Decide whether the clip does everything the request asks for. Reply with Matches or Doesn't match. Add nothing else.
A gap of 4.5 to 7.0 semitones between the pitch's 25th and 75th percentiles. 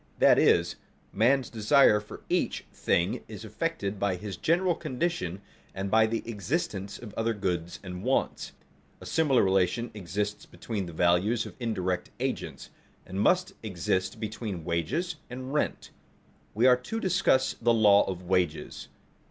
Matches